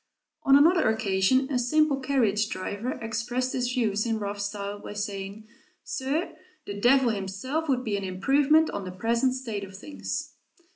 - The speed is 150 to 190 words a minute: Yes, average, 160 wpm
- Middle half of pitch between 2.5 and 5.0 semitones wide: Yes, average, 4.6 semitones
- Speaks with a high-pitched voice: Yes, high, 225 Hz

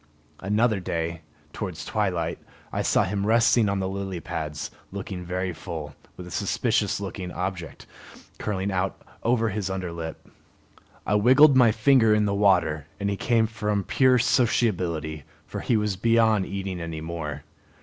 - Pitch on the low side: Yes, low, 100 Hz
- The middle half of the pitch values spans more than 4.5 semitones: No, average, 3.9 semitones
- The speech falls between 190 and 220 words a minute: No, average, 155 wpm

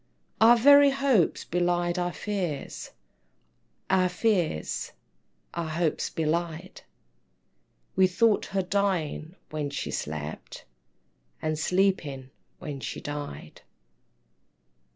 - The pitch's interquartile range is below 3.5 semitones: No, average, 4.2 semitones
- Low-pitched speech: No, medium, 175 Hz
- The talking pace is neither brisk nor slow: No, slow, 90 wpm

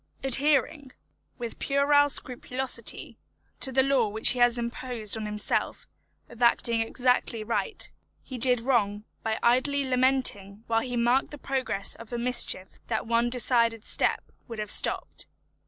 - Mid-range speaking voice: No, high, 240 Hz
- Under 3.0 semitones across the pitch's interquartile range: Yes, narrow, 2.5 semitones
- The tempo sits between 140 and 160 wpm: Yes, average, 145 wpm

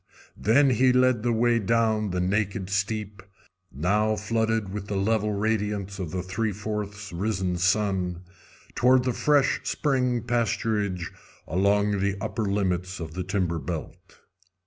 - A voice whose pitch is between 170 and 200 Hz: No, low, 105 Hz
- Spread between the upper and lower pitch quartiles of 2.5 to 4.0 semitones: Yes, average, 3.1 semitones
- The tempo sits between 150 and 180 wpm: No, average, 140 wpm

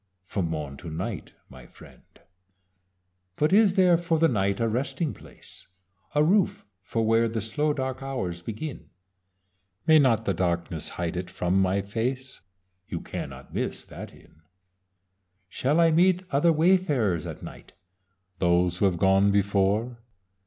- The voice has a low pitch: Yes, low, 115 Hz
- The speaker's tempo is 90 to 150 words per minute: Yes, average, 145 wpm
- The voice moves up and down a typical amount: No, wide, 8.4 semitones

